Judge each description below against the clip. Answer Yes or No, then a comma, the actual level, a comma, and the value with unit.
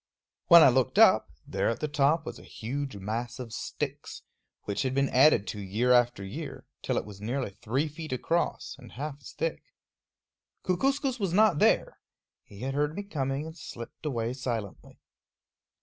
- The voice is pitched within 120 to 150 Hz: Yes, low, 135 Hz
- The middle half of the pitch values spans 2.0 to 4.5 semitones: No, average, 5.0 semitones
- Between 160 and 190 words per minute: Yes, average, 175 wpm